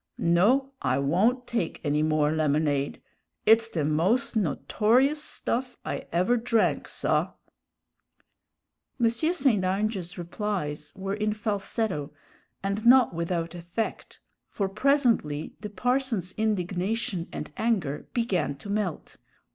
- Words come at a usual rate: No, slow, 115 wpm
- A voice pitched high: Yes, high, 200 Hz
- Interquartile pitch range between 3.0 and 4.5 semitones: No, wide, 5.6 semitones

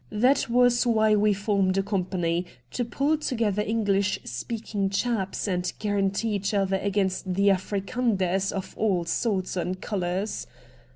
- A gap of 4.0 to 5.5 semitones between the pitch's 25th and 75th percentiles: No, narrow, 2.6 semitones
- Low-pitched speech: No, high, 200 Hz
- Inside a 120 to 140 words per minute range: Yes, slow, 135 wpm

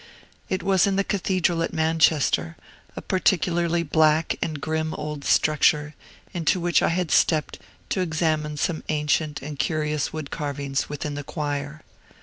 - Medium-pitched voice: Yes, medium, 155 Hz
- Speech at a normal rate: Yes, average, 145 wpm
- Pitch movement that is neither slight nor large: No, narrow, 2.3 semitones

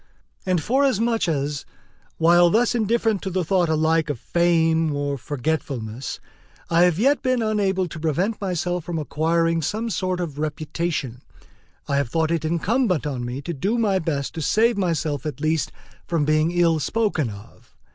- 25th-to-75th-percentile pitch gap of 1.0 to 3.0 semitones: No, average, 4.2 semitones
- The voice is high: No, medium, 165 Hz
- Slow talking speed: No, average, 165 wpm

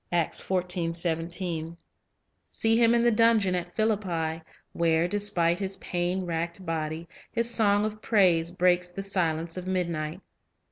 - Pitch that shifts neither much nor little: Yes, average, 3.6 semitones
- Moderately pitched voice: Yes, medium, 180 Hz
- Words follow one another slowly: Yes, slow, 130 wpm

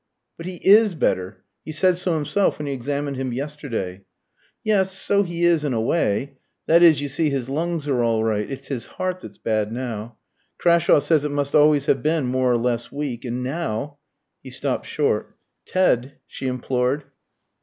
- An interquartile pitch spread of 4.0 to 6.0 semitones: Yes, average, 5.1 semitones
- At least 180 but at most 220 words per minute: Yes, average, 190 wpm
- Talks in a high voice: No, medium, 140 Hz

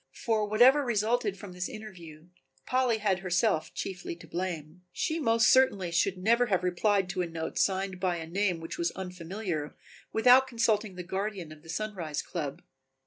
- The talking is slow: No, average, 170 wpm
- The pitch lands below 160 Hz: No, high, 190 Hz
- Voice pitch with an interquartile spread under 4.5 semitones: Yes, average, 3.9 semitones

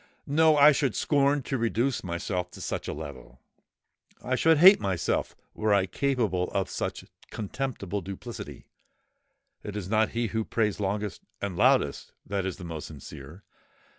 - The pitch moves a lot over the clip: Yes, wide, 6.0 semitones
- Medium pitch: No, low, 105 Hz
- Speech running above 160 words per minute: No, average, 145 wpm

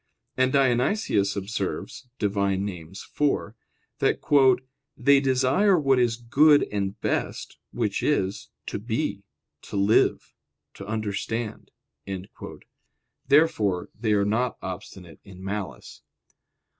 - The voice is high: No, low, 110 Hz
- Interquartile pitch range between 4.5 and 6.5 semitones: Yes, average, 5.1 semitones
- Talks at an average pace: No, slow, 105 wpm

